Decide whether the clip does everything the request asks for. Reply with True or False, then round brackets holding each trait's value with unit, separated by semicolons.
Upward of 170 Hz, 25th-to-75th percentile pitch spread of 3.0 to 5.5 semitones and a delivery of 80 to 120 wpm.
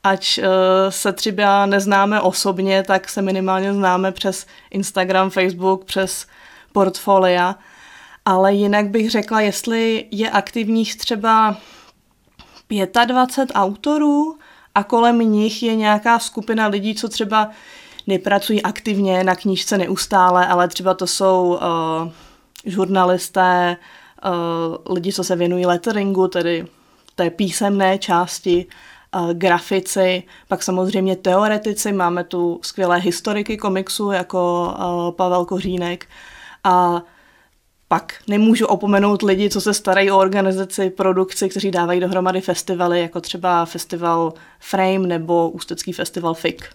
False (190 Hz; 2.4 semitones; 115 wpm)